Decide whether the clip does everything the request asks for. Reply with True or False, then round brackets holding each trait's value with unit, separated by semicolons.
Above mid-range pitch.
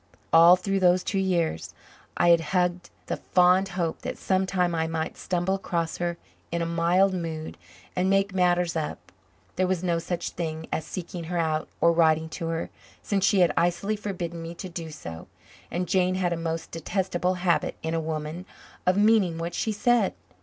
False (175 Hz)